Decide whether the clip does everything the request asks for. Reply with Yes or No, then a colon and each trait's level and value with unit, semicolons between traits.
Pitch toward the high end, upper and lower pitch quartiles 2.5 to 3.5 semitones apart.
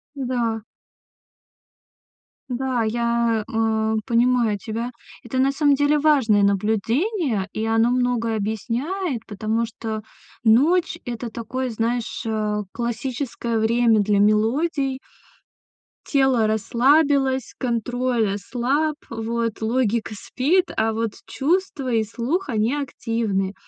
Yes: high, 235 Hz; average, 3.1 semitones